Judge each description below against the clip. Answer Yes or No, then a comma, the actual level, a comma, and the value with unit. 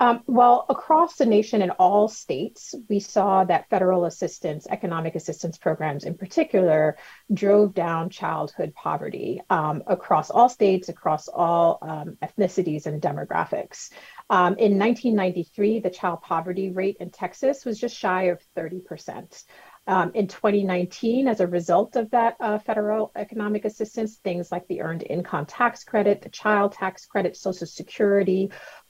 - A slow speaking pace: No, average, 145 wpm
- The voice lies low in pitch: No, high, 195 Hz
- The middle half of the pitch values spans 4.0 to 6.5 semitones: No, average, 3.6 semitones